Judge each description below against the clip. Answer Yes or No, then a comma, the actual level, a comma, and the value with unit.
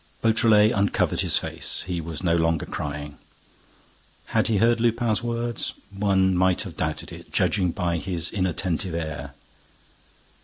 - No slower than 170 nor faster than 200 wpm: No, average, 140 wpm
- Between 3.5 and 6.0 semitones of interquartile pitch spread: Yes, average, 4.5 semitones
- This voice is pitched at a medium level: No, very low, 95 Hz